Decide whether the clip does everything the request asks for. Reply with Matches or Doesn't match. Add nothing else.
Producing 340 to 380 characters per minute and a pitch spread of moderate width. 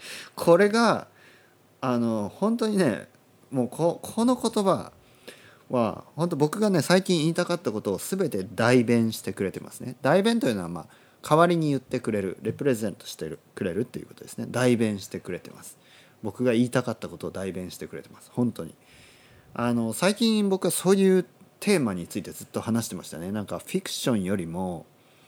Doesn't match